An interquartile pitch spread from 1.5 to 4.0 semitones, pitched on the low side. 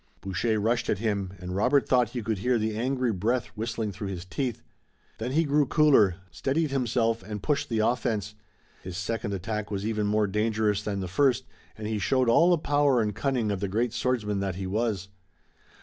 Yes: average, 3.7 semitones; low, 110 Hz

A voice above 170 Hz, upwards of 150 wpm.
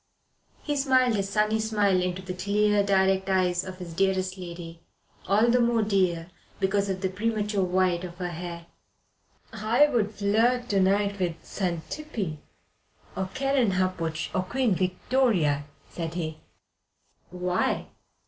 No: high, 190 Hz; slow, 135 wpm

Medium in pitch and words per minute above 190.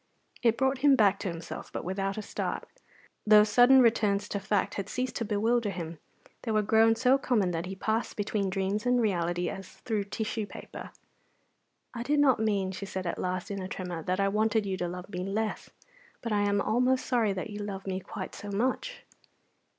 No: high, 205 Hz; fast, 205 wpm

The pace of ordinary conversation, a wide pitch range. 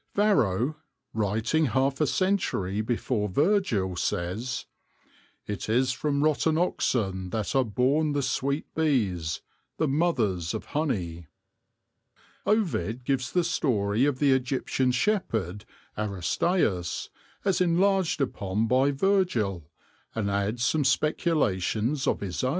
No: slow, 120 wpm; wide, 7.1 semitones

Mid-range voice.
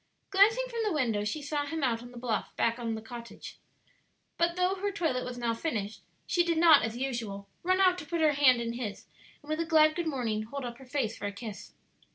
No: very high, 265 Hz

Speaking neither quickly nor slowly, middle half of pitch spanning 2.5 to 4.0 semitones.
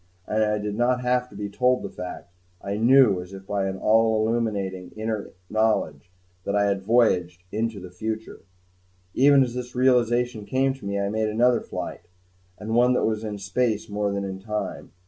Yes: average, 185 wpm; average, 3.3 semitones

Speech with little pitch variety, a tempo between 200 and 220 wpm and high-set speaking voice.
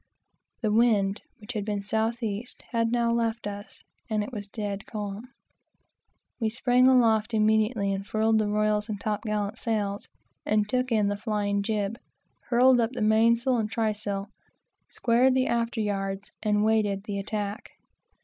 No: narrow, 2.1 semitones; average, 160 wpm; high, 215 Hz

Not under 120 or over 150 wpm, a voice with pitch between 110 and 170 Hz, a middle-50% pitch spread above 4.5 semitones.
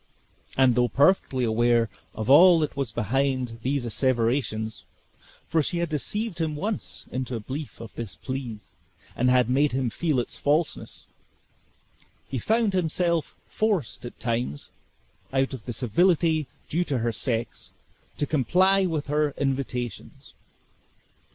Yes: average, 140 wpm; low, 135 Hz; average, 4.9 semitones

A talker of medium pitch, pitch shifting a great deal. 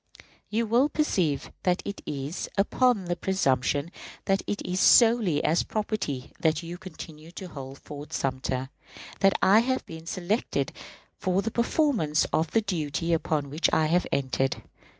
Yes: medium, 175 Hz; wide, 5.7 semitones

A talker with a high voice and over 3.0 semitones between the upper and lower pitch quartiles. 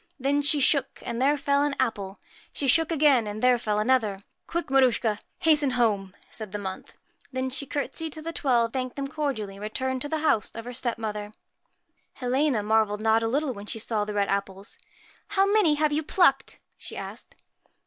Yes: very high, 255 Hz; average, 5.2 semitones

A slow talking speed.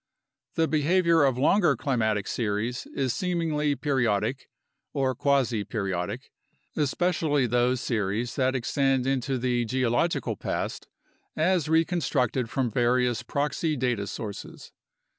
Yes: slow, 110 wpm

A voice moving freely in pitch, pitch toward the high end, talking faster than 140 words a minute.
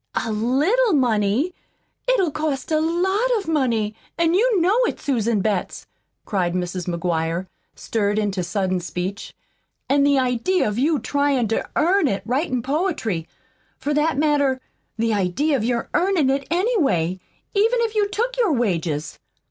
Yes: wide, 8.6 semitones; very high, 270 Hz; average, 150 wpm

